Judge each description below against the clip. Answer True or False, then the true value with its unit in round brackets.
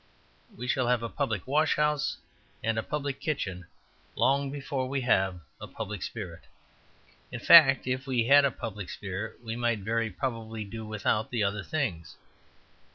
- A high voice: False (120 Hz)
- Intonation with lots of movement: False (4.2 semitones)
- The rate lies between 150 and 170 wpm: True (160 wpm)